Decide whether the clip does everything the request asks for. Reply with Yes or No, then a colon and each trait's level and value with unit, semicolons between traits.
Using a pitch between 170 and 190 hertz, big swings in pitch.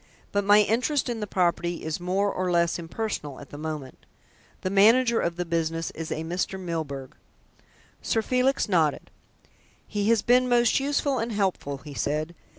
Yes: medium, 185 Hz; wide, 5.7 semitones